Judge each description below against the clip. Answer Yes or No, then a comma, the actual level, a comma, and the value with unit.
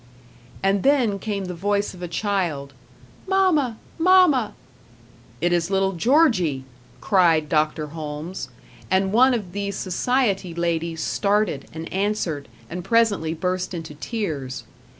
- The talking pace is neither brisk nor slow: No, slow, 125 wpm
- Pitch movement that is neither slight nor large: Yes, average, 4.6 semitones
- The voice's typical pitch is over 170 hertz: Yes, high, 190 Hz